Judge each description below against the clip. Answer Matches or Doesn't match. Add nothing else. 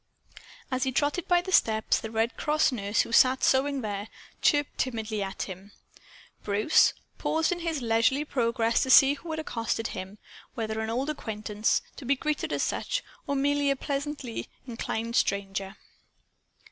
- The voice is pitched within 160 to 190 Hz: Doesn't match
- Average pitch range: Matches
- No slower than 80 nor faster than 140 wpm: Doesn't match